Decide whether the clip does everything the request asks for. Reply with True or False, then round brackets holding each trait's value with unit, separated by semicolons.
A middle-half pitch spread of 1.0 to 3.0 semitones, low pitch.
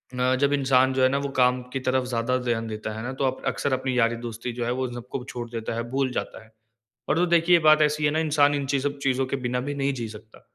True (2.7 semitones; 130 Hz)